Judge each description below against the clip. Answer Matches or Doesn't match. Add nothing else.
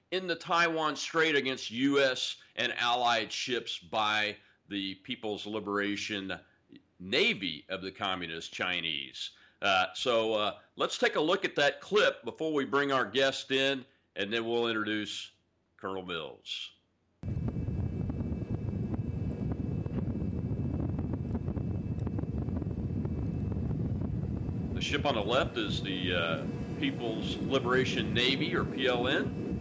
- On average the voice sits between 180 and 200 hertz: Doesn't match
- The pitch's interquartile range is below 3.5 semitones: Doesn't match